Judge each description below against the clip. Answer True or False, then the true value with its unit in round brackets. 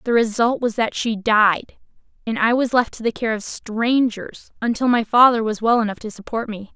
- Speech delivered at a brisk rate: True (215 wpm)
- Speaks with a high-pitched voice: True (225 Hz)